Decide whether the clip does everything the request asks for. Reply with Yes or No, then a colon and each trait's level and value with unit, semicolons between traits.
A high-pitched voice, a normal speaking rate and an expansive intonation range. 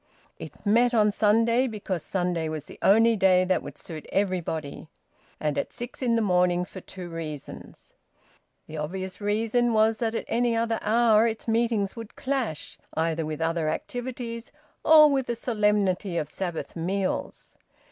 No: high, 205 Hz; average, 155 wpm; average, 4.8 semitones